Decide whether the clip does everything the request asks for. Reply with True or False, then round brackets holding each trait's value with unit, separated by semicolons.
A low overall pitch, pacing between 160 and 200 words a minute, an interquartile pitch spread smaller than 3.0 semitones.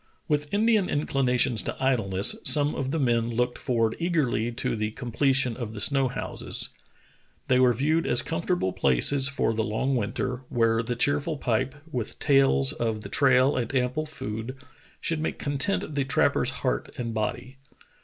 False (125 Hz; 165 wpm; 3.9 semitones)